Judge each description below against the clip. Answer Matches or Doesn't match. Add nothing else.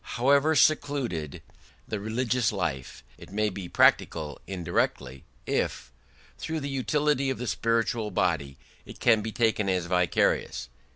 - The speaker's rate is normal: Doesn't match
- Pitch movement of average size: Doesn't match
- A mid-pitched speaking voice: Doesn't match